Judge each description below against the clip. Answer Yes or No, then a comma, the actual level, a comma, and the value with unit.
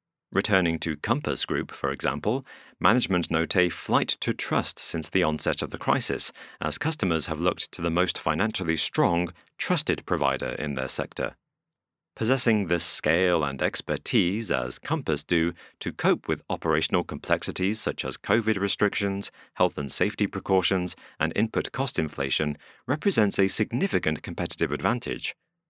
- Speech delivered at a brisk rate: No, average, 145 wpm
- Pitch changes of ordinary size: Yes, average, 4.2 semitones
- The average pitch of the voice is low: Yes, very low, 90 Hz